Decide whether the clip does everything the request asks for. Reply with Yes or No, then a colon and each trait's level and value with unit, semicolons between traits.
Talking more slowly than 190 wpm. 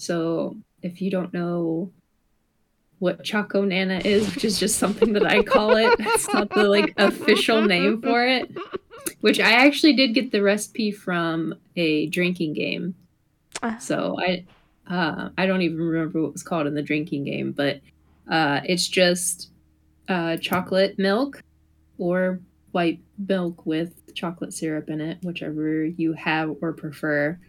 Yes: average, 155 wpm